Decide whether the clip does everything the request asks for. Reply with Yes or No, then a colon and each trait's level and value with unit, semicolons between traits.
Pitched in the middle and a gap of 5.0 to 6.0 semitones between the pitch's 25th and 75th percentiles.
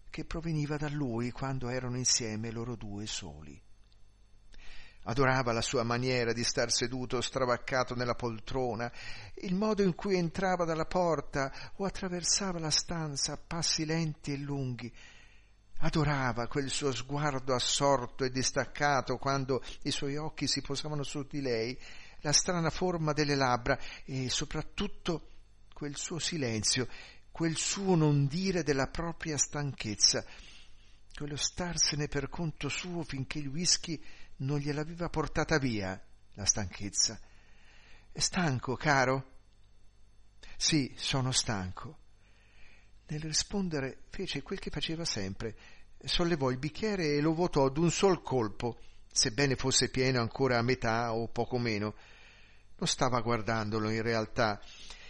No: low, 130 Hz; average, 5.3 semitones